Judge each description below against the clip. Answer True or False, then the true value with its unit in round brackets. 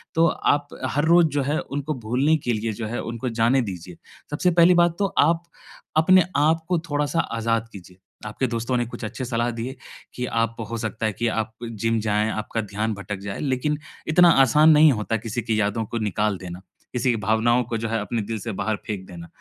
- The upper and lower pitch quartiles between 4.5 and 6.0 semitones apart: True (5.0 semitones)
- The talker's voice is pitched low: True (115 Hz)